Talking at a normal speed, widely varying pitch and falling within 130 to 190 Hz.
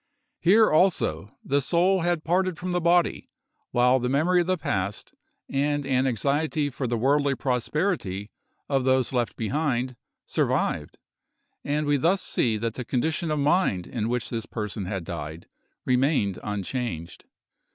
Yes: average, 150 wpm; wide, 5.8 semitones; low, 135 Hz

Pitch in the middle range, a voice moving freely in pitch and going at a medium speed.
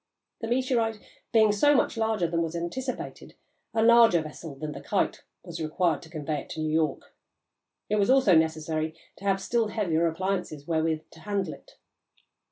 Yes: medium, 175 Hz; wide, 5.8 semitones; average, 175 wpm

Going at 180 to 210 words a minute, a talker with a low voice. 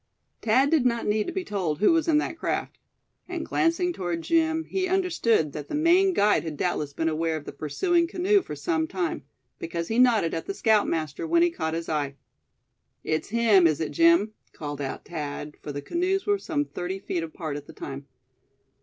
No: average, 200 wpm; high, 205 Hz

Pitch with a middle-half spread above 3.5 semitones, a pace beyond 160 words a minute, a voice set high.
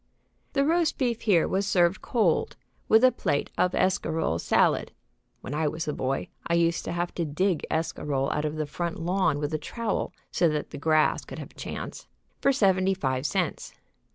No: average, 4.3 semitones; average, 190 wpm; medium, 170 Hz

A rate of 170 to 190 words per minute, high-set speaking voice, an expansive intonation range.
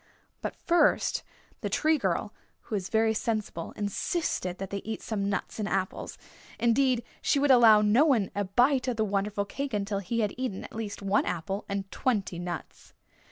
No: average, 180 wpm; high, 210 Hz; average, 3.4 semitones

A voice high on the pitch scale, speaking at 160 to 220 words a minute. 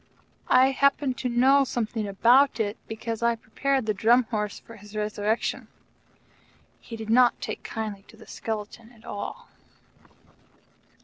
No: high, 225 Hz; average, 140 wpm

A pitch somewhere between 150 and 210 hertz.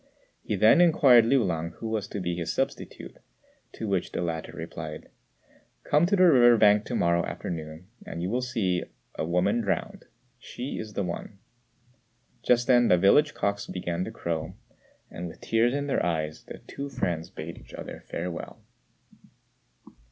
No: low, 100 Hz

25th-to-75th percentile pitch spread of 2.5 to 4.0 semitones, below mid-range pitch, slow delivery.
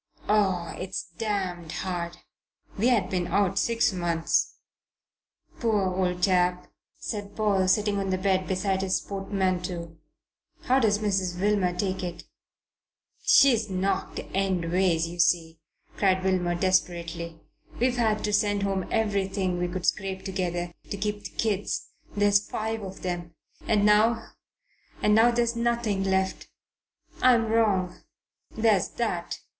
No: average, 2.8 semitones; high, 190 Hz; slow, 130 wpm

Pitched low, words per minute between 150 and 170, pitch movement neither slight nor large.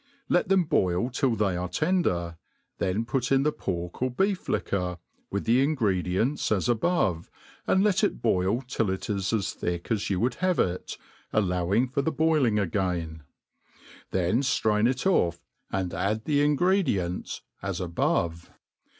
No: low, 105 Hz; average, 155 wpm; wide, 6.9 semitones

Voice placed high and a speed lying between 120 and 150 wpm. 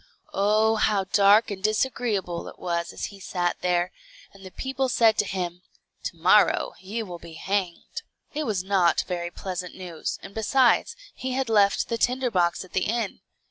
No: high, 195 Hz; average, 180 wpm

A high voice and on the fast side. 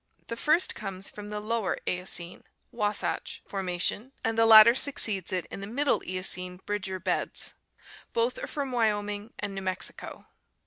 No: high, 205 Hz; average, 150 wpm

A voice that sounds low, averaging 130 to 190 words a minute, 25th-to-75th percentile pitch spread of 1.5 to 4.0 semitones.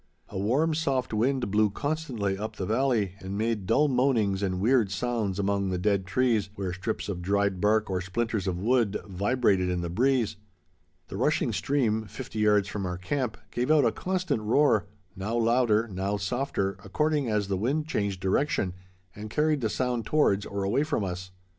No: low, 105 Hz; average, 180 wpm; average, 4.6 semitones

